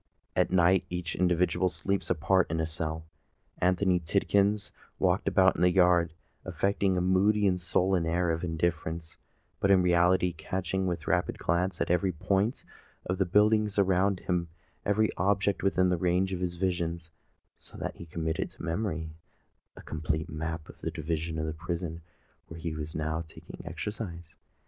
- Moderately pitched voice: No, very low, 90 Hz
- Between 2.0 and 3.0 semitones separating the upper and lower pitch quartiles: Yes, narrow, 2.5 semitones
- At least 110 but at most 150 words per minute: No, average, 160 wpm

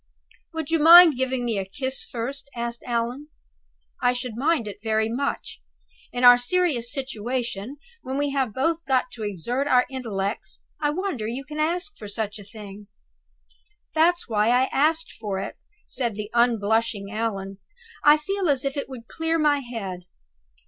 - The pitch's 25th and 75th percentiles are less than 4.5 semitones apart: No, average, 4.8 semitones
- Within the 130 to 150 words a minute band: No, average, 165 wpm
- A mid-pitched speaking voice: No, high, 245 Hz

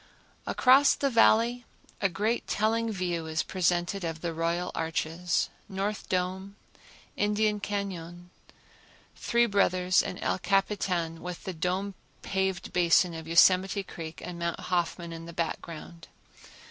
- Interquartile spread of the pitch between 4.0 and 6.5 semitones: No, average, 2.9 semitones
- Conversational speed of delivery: No, slow, 130 wpm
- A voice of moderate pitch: Yes, medium, 180 Hz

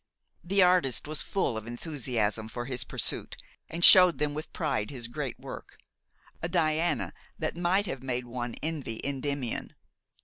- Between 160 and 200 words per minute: No, average, 150 wpm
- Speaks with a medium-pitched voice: Yes, medium, 145 Hz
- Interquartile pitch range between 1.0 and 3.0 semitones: No, wide, 5.5 semitones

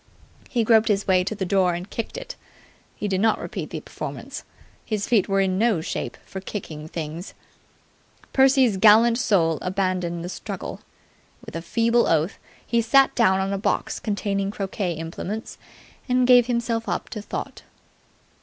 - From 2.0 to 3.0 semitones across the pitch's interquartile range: No, average, 3.8 semitones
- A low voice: No, high, 200 Hz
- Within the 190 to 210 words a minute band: No, average, 165 wpm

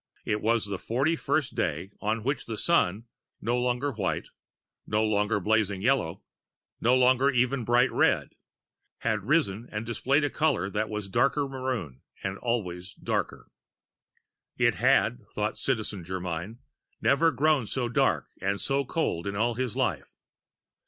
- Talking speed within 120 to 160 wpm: Yes, average, 150 wpm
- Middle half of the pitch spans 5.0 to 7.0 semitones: No, average, 4.5 semitones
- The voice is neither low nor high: No, low, 115 Hz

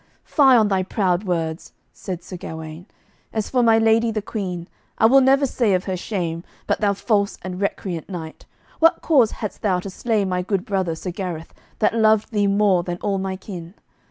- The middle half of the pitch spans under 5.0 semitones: Yes, average, 3.6 semitones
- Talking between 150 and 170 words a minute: No, average, 195 wpm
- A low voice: No, high, 195 Hz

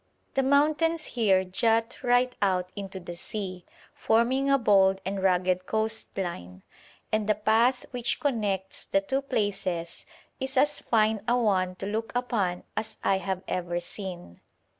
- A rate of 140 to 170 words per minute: Yes, average, 150 wpm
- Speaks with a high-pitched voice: Yes, high, 210 Hz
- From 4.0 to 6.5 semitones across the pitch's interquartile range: Yes, average, 4.5 semitones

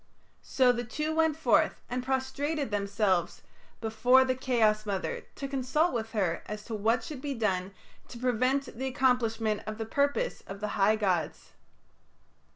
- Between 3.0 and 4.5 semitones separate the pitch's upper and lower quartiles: Yes, average, 3.8 semitones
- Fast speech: No, average, 160 wpm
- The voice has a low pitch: No, high, 240 Hz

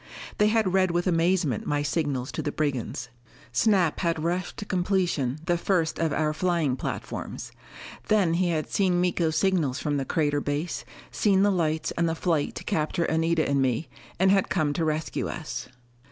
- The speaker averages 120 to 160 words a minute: No, average, 180 wpm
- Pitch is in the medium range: Yes, medium, 165 Hz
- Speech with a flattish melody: No, average, 3.6 semitones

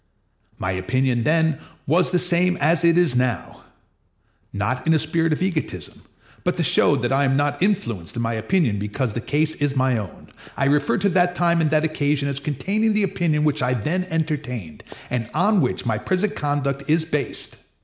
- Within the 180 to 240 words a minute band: Yes, average, 190 wpm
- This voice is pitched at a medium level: Yes, medium, 150 Hz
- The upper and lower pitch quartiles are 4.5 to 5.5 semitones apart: Yes, average, 5.1 semitones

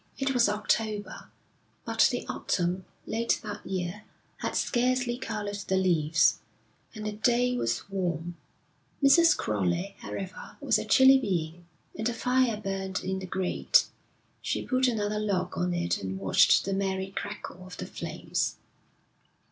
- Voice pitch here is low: No, high, 195 Hz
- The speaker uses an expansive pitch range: No, average, 4.3 semitones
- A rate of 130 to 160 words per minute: Yes, average, 145 wpm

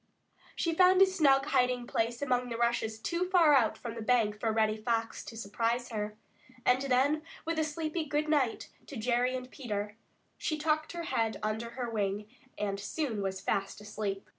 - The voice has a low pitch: No, high, 240 Hz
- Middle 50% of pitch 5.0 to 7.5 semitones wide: Yes, wide, 5.4 semitones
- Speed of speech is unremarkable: Yes, average, 185 wpm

